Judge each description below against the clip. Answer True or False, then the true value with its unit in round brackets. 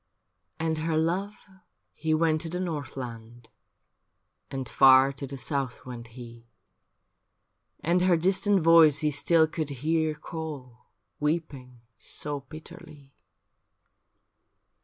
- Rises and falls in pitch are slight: False (4.0 semitones)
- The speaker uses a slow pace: True (115 wpm)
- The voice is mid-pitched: True (150 Hz)